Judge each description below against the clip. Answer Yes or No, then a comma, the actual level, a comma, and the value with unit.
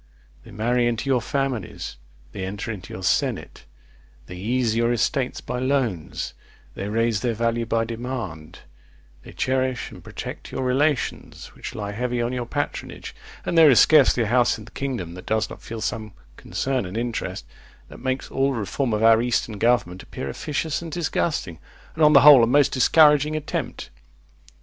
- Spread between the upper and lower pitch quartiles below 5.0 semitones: Yes, average, 3.5 semitones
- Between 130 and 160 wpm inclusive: No, average, 175 wpm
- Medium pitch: No, low, 120 Hz